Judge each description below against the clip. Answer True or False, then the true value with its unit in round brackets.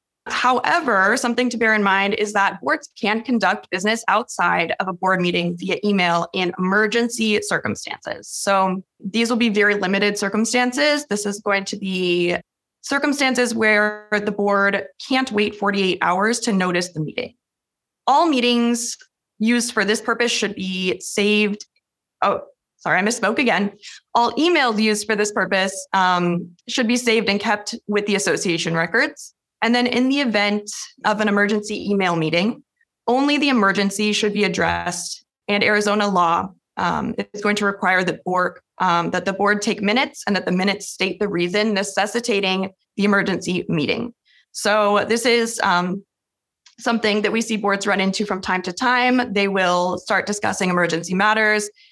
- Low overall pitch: False (205 Hz)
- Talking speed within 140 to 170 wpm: True (160 wpm)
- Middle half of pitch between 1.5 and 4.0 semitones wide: True (3.4 semitones)